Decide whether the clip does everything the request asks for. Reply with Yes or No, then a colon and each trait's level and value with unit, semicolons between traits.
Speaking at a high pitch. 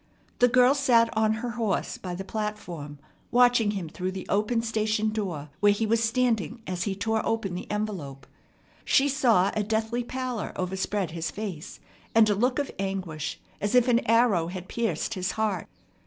Yes: high, 215 Hz